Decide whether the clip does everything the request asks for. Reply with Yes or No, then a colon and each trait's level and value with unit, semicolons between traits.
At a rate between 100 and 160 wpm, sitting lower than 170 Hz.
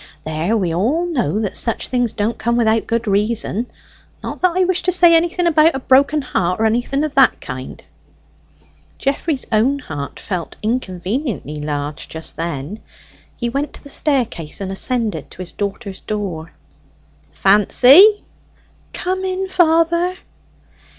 No: average, 145 wpm; high, 235 Hz